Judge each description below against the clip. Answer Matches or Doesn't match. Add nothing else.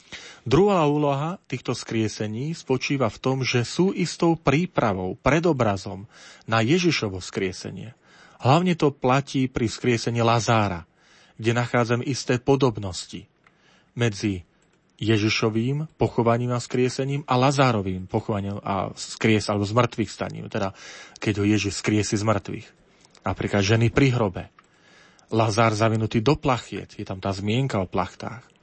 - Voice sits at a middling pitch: Doesn't match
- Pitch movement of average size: Matches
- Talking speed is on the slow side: Doesn't match